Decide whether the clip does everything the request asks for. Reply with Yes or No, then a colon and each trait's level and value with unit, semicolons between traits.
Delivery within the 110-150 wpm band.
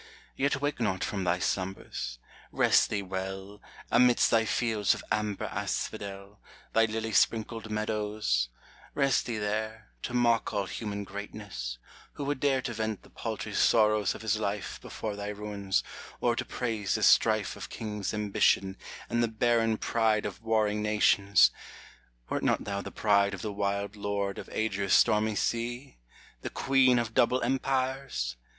No: average, 160 wpm